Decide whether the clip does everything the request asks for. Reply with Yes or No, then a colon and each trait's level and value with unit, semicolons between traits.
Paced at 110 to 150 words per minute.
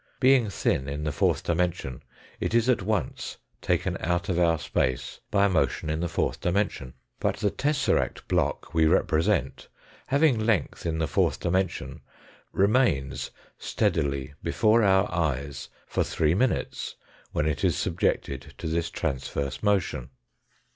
Yes: average, 145 wpm